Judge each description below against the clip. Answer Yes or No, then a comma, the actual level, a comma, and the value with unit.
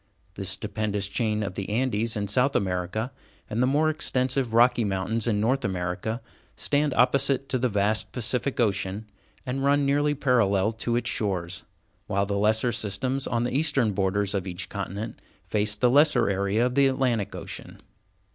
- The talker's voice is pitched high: No, low, 110 Hz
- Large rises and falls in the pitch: No, average, 4.2 semitones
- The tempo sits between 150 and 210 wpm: Yes, average, 165 wpm